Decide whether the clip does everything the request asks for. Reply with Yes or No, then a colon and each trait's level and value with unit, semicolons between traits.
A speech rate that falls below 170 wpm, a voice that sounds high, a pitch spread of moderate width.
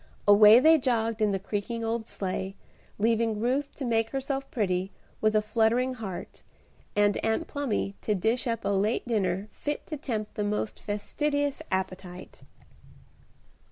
Yes: average, 150 wpm; high, 220 Hz; average, 3.4 semitones